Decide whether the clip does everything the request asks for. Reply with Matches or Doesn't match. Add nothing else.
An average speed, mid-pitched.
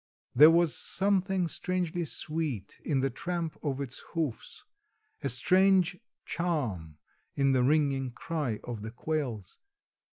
Doesn't match